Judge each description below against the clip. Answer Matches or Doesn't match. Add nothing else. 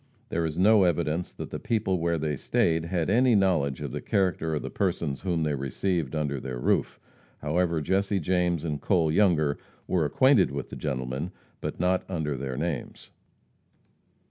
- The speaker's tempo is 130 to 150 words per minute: Doesn't match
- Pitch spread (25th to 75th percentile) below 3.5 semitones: Doesn't match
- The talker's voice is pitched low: Matches